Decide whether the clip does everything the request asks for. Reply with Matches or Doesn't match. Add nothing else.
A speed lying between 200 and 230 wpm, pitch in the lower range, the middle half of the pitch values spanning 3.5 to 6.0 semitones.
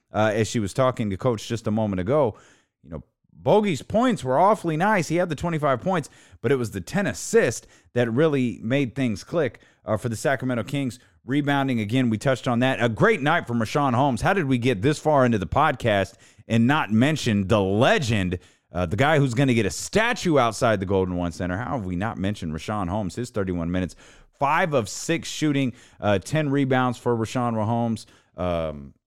Matches